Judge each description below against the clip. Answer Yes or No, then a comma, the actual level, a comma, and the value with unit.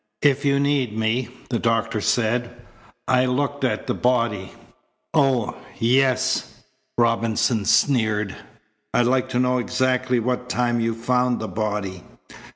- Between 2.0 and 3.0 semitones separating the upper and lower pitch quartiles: Yes, narrow, 2.4 semitones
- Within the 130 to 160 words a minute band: Yes, slow, 135 wpm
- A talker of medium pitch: No, low, 120 Hz